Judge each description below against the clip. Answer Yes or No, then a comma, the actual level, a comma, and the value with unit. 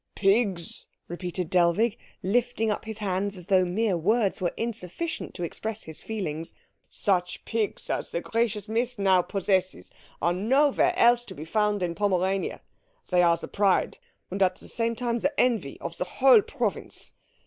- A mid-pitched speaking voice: No, high, 200 Hz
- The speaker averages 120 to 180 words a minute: Yes, average, 165 wpm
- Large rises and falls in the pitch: No, average, 4.1 semitones